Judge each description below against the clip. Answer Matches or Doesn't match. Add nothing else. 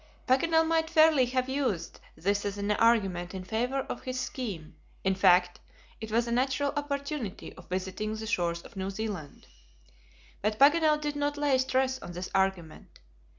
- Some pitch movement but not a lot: Doesn't match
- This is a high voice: Matches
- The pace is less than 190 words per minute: Matches